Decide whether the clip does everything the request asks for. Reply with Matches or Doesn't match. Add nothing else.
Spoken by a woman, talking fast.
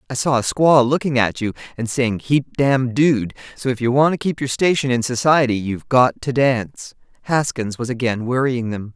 Matches